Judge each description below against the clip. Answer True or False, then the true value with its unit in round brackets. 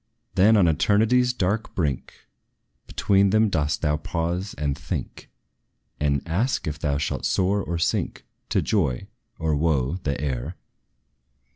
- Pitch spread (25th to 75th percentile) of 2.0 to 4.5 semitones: False (5.3 semitones)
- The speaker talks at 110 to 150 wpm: True (135 wpm)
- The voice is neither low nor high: False (85 Hz)